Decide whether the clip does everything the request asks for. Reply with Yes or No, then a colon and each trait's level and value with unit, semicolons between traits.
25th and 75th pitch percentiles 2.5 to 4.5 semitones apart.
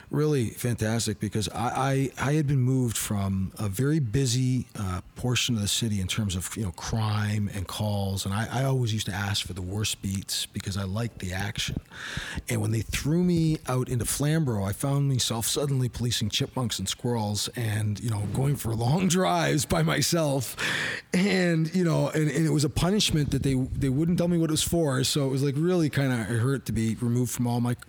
No: average, 5.2 semitones